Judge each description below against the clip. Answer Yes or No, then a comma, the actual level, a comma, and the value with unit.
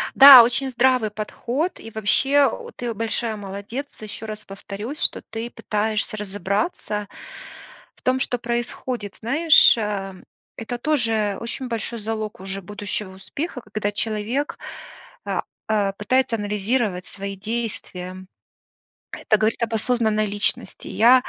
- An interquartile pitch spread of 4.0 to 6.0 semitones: No, average, 2.9 semitones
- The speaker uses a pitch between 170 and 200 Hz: No, high, 220 Hz